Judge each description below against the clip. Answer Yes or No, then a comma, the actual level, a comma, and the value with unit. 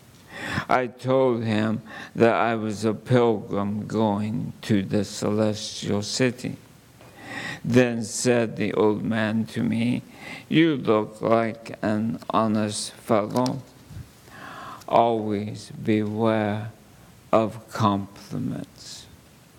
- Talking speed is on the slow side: Yes, slow, 90 wpm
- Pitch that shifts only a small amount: Yes, narrow, 1.7 semitones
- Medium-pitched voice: No, low, 110 Hz